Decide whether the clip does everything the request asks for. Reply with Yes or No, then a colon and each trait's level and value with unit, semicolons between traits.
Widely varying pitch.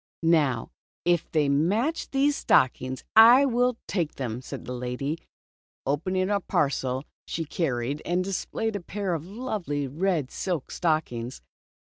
Yes: wide, 6.6 semitones